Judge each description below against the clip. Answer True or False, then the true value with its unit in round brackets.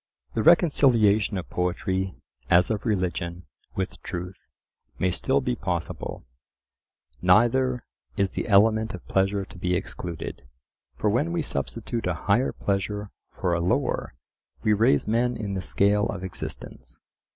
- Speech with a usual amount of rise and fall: True (4.0 semitones)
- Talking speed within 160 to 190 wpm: False (140 wpm)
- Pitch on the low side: True (100 Hz)